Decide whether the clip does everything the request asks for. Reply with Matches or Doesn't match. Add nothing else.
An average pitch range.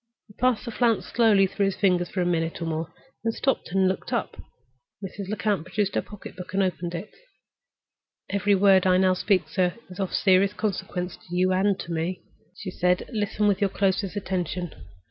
Doesn't match